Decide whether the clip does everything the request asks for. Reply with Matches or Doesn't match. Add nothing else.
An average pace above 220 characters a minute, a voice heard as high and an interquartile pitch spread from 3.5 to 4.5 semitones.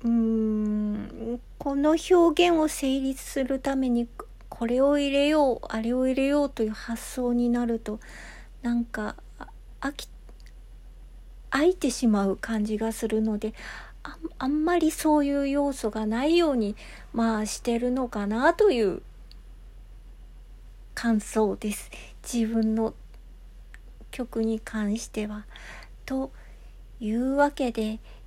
Doesn't match